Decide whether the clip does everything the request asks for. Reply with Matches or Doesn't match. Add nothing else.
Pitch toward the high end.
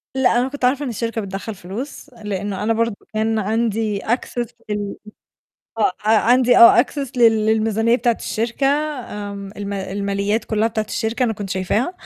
Matches